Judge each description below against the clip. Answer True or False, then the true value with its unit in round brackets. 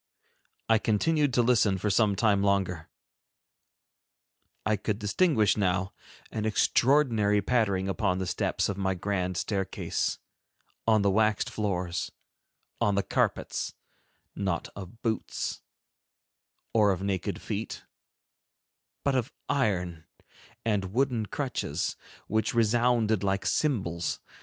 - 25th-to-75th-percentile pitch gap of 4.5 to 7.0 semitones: False (3.1 semitones)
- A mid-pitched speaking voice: False (105 Hz)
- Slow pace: True (115 wpm)